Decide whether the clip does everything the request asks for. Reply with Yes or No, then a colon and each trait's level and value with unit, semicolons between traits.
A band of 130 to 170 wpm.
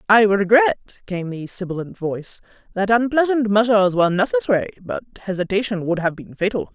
Yes: average, 150 wpm